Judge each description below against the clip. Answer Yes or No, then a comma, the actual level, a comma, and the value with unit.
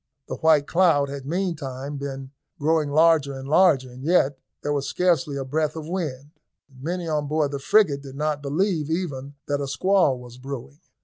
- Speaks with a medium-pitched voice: Yes, medium, 145 Hz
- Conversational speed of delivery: Yes, average, 180 wpm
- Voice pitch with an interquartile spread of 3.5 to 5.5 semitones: No, average, 2.8 semitones